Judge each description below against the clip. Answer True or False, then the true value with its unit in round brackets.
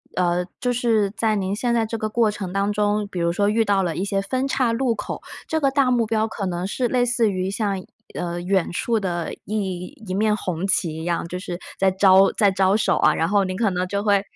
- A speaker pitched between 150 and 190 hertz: False (200 Hz)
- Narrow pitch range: False (3.2 semitones)